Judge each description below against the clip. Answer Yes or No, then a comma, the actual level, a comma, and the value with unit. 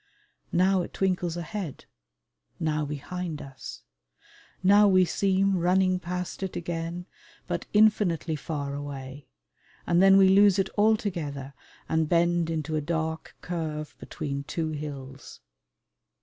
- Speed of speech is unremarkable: No, slow, 120 wpm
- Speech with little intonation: No, average, 3.7 semitones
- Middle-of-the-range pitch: Yes, medium, 170 Hz